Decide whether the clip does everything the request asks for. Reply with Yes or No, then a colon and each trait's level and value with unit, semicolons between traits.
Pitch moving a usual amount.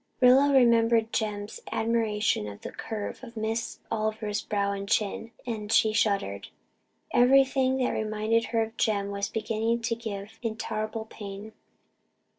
No: narrow, 1.8 semitones